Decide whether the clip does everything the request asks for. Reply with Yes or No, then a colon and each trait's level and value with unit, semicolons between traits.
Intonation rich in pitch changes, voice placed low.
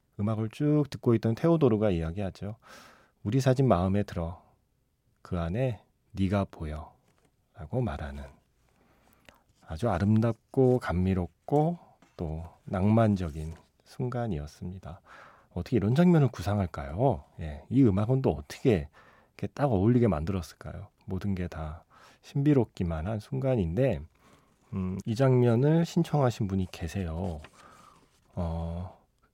Yes: wide, 6.5 semitones; low, 100 Hz